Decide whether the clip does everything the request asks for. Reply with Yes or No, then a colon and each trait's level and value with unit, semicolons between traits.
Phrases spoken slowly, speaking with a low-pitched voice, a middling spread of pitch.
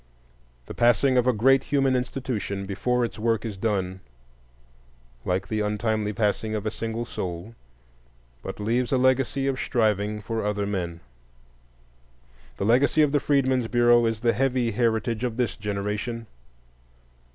No: average, 145 wpm; low, 115 Hz; average, 3.2 semitones